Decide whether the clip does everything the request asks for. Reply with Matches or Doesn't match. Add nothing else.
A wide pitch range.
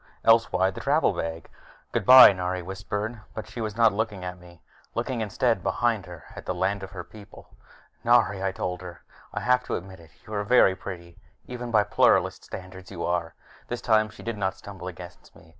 Doesn't match